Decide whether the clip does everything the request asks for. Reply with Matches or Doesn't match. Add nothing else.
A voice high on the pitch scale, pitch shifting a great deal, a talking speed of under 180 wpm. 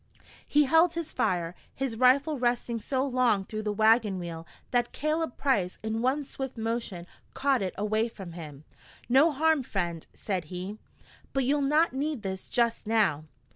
Matches